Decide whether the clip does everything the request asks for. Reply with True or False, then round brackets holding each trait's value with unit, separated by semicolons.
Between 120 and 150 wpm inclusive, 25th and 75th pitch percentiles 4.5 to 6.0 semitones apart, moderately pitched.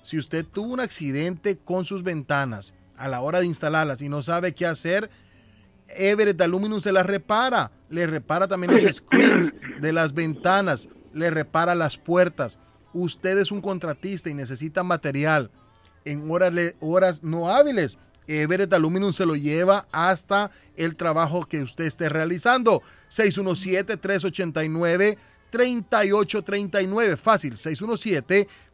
False (130 wpm; 3.9 semitones; 175 Hz)